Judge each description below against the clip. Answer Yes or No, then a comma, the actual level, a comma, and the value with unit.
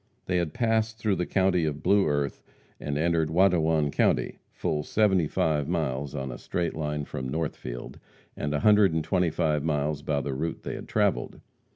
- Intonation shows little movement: No, average, 3.5 semitones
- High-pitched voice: No, very low, 80 Hz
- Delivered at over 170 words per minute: Yes, average, 185 wpm